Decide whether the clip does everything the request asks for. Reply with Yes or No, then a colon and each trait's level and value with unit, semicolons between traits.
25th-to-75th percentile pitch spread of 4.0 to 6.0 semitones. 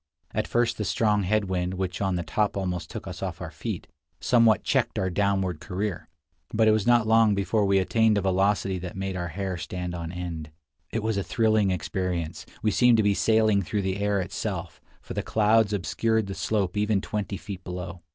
No: average, 2.8 semitones